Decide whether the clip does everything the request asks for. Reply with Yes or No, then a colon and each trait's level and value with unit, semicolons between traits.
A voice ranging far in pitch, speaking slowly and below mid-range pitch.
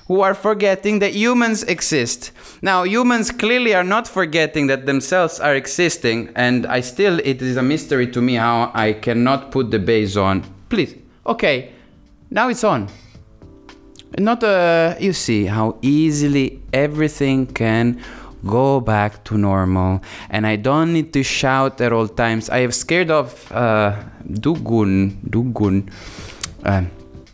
No: wide, 7.0 semitones; average, 145 wpm; low, 125 Hz